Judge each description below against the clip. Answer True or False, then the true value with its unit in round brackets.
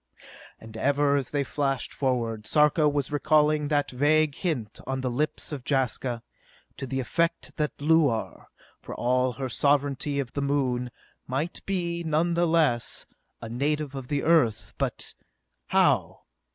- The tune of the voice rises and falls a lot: False (3.1 semitones)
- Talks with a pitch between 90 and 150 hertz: True (140 Hz)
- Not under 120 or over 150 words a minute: True (140 wpm)